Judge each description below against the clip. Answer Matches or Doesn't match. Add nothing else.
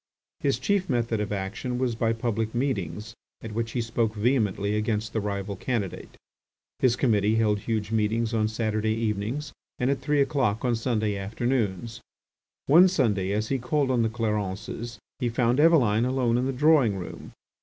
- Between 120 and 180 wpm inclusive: Matches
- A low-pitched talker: Matches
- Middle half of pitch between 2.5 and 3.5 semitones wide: Matches